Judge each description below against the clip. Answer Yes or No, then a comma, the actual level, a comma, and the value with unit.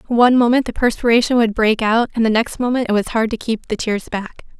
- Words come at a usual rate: No, fast, 250 wpm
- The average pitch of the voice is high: Yes, high, 230 Hz